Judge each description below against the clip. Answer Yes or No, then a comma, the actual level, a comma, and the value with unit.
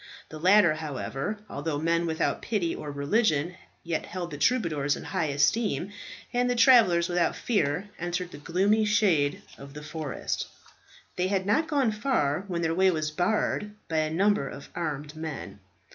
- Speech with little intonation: No, average, 5.3 semitones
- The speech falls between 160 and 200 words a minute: Yes, average, 165 wpm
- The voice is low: No, medium, 170 Hz